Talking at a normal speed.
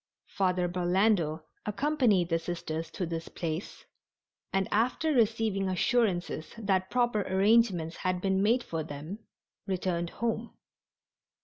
No: slow, 115 wpm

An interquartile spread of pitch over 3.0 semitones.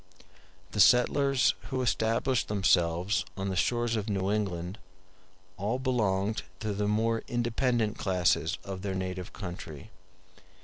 Yes: average, 3.7 semitones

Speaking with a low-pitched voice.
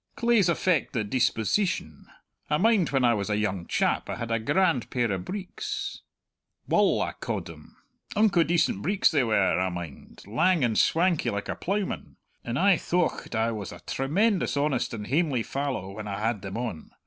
Yes: low, 130 Hz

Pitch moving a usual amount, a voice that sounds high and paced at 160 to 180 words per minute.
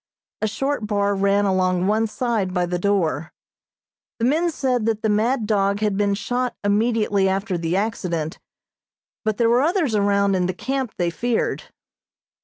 Yes: average, 3.2 semitones; high, 205 Hz; average, 165 wpm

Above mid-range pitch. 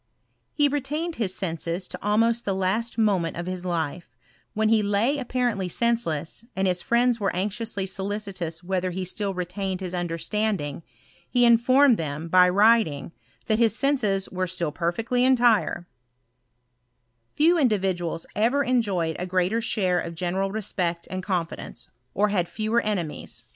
Yes: high, 195 Hz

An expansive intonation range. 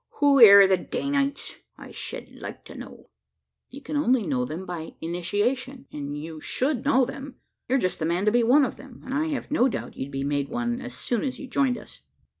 Yes: wide, 7.5 semitones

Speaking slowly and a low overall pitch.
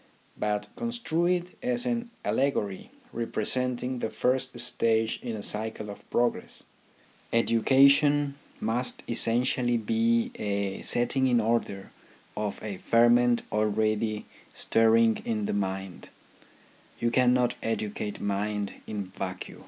Yes: slow, 115 wpm; low, 115 Hz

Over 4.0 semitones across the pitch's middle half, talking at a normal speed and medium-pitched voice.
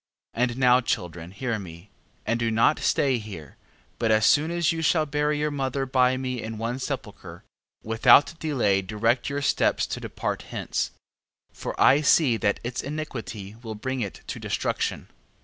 No: average, 4.4 semitones; average, 175 wpm; low, 125 Hz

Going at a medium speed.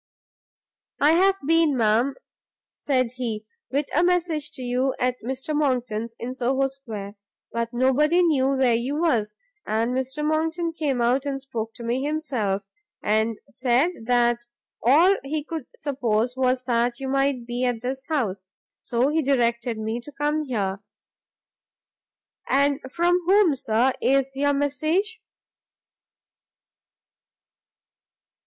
No: slow, 130 wpm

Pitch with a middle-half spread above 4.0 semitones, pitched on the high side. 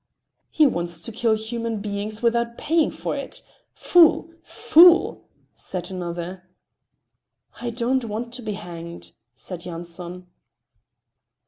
Yes: average, 5.1 semitones; high, 215 Hz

